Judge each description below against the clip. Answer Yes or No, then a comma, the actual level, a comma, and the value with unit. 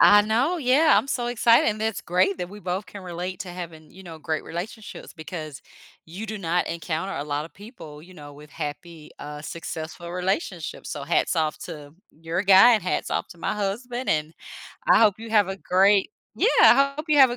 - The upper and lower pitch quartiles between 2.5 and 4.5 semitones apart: No, average, 5.1 semitones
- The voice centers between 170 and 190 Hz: Yes, medium, 185 Hz